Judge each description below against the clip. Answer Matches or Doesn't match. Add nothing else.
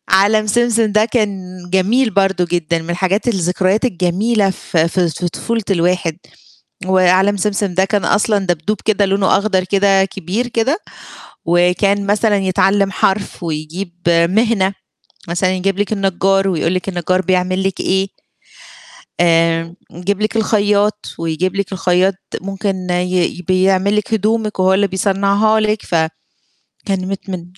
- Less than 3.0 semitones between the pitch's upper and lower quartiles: Matches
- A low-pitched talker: Doesn't match